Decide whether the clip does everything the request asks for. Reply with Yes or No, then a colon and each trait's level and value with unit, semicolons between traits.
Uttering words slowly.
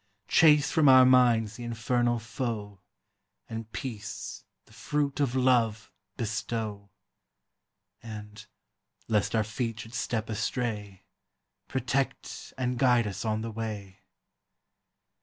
Yes: slow, 110 wpm